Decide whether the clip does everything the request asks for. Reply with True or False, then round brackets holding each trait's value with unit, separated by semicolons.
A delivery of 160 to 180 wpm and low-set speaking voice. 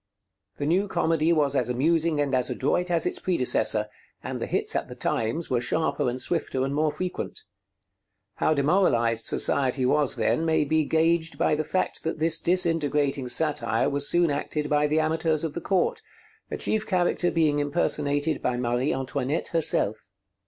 False (170 wpm; 150 Hz)